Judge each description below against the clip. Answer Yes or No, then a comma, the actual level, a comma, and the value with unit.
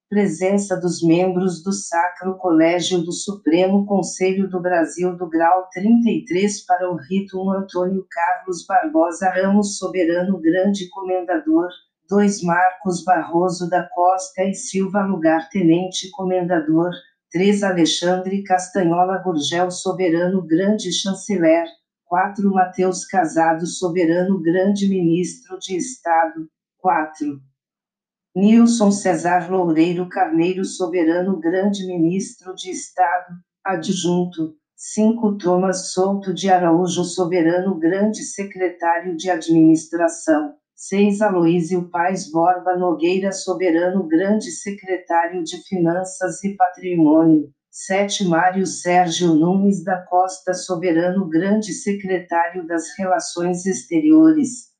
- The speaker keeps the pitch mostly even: Yes, narrow, 2.2 semitones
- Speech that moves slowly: Yes, slow, 105 wpm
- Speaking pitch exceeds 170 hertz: Yes, medium, 185 Hz